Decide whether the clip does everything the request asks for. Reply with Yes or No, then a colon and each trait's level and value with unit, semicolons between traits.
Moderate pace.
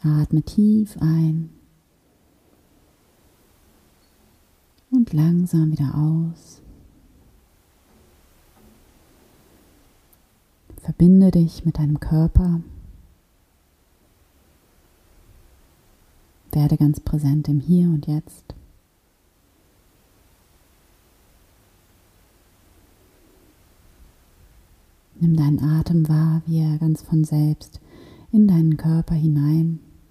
No: slow, 65 wpm